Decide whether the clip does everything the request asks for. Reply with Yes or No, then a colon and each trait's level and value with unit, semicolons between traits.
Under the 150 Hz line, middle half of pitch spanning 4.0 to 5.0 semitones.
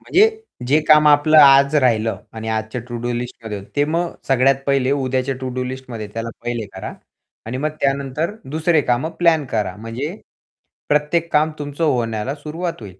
Yes: low, 135 Hz; average, 4.3 semitones